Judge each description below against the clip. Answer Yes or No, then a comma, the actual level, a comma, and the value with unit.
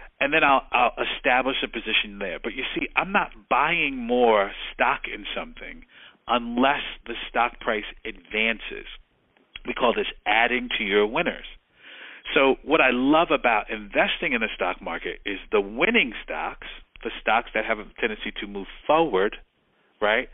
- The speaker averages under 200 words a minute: Yes, average, 160 wpm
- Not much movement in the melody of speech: No, average, 4.2 semitones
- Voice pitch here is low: Yes, low, 115 Hz